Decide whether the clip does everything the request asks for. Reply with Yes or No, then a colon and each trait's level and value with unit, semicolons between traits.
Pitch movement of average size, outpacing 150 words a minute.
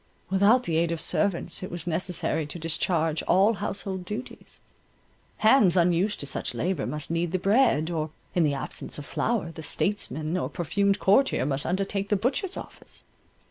Yes: average, 3.8 semitones; average, 170 wpm